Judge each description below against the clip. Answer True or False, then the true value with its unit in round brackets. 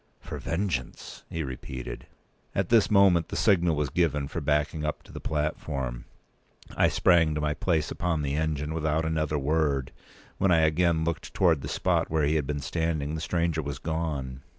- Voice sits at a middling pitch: False (80 Hz)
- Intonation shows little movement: True (2.3 semitones)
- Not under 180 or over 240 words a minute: True (185 wpm)